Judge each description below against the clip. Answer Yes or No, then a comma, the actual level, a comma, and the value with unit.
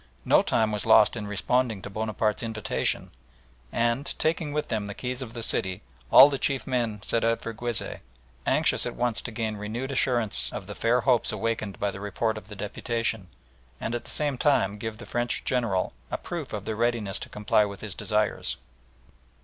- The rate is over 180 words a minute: Yes, average, 195 wpm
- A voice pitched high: No, low, 115 Hz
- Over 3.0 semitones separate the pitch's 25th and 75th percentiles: No, narrow, 2.5 semitones